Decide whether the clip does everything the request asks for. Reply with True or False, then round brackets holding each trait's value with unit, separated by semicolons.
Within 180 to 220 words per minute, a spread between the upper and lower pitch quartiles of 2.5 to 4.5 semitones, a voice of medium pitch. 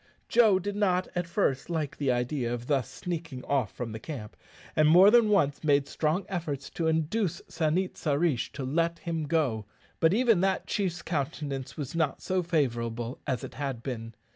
False (190 wpm; 5.0 semitones; 155 Hz)